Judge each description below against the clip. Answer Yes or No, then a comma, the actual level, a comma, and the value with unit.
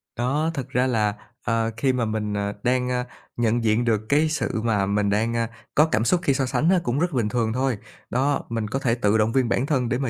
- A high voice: No, low, 120 Hz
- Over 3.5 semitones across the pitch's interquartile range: No, average, 3.2 semitones